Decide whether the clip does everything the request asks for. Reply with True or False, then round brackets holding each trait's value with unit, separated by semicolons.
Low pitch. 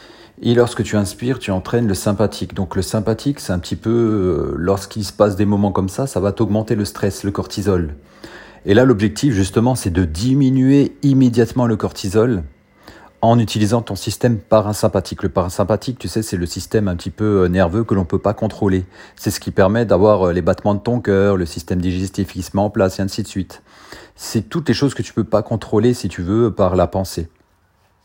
True (105 Hz)